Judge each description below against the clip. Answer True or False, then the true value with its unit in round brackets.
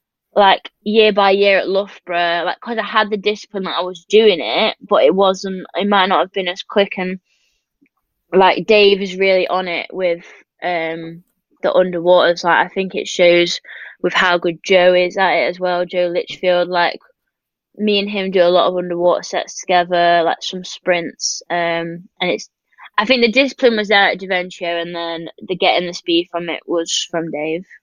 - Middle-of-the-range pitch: True (180 Hz)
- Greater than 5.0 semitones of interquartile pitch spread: False (2.4 semitones)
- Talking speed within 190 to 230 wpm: True (195 wpm)